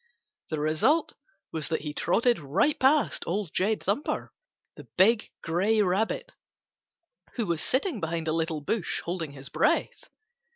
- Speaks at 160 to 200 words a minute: No, average, 140 wpm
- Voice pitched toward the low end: No, medium, 180 Hz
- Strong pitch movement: Yes, wide, 5.7 semitones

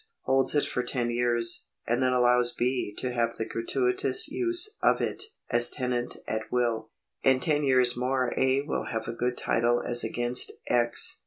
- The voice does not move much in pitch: Yes, narrow, 1.6 semitones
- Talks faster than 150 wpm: Yes, average, 175 wpm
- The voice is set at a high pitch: No, low, 125 Hz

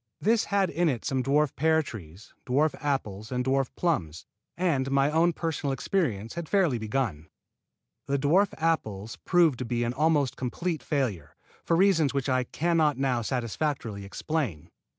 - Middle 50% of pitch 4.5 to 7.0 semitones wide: Yes, average, 5.2 semitones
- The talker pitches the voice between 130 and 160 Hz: Yes, medium, 140 Hz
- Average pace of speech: Yes, average, 160 wpm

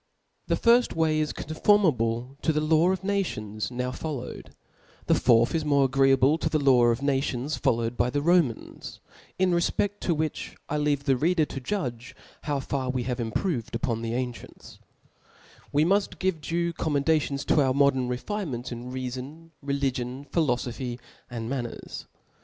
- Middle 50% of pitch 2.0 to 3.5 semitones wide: No, average, 4.3 semitones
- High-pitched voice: No, medium, 140 Hz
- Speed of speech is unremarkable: Yes, average, 160 wpm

